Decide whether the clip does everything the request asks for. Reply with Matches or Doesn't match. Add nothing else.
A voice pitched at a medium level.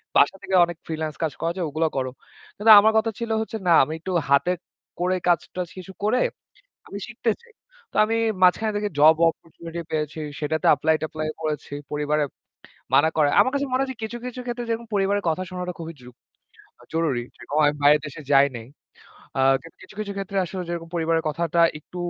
Matches